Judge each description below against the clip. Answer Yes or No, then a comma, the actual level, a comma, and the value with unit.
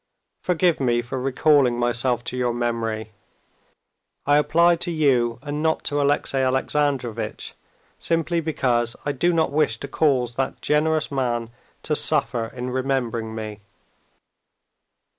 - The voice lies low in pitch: Yes, low, 130 Hz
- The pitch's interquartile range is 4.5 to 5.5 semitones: No, average, 3.9 semitones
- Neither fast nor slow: No, slow, 130 wpm